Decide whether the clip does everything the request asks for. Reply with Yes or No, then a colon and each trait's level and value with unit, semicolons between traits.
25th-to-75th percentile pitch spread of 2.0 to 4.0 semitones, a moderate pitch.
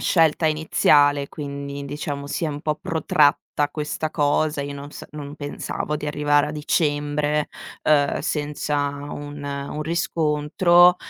No: narrow, 1.1 semitones; medium, 150 Hz